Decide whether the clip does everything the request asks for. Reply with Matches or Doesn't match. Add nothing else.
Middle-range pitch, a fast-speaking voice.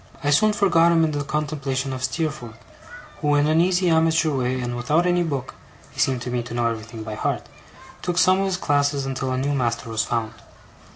Matches